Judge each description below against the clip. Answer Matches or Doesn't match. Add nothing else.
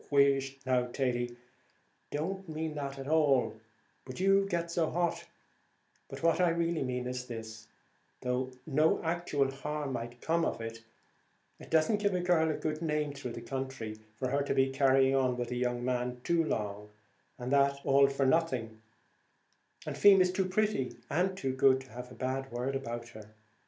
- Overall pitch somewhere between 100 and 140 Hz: Matches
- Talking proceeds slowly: Doesn't match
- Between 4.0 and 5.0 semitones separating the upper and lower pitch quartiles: Matches